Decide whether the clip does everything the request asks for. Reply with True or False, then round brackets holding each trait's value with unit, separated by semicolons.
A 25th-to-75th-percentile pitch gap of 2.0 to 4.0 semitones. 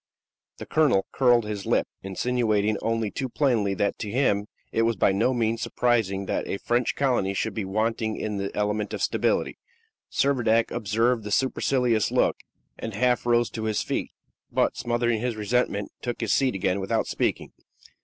True (2.9 semitones)